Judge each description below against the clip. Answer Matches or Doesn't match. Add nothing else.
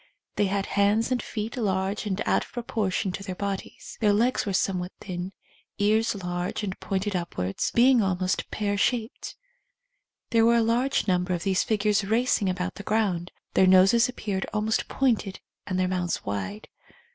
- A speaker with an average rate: Matches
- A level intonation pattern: Doesn't match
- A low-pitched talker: Doesn't match